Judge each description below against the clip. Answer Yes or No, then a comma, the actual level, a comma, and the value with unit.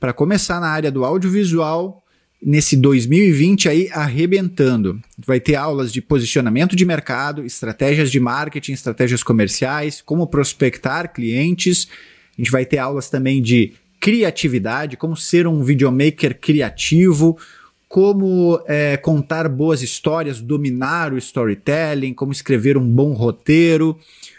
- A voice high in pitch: No, medium, 150 Hz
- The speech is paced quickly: No, average, 125 wpm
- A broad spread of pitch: No, average, 3.8 semitones